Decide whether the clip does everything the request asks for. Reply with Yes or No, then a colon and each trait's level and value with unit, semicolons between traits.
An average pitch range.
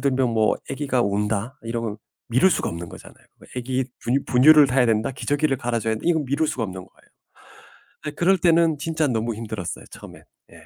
Yes: average, 4.7 semitones